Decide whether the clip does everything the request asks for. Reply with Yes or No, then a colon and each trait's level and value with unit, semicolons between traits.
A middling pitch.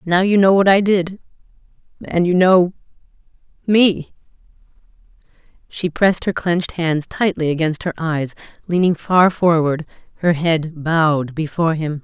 Yes: medium, 170 Hz